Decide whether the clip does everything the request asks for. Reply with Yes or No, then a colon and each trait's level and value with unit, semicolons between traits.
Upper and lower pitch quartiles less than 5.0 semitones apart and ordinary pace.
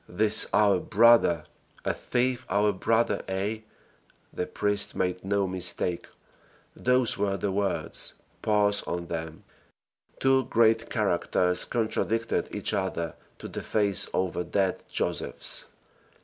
No: average, 3.2 semitones; slow, 120 wpm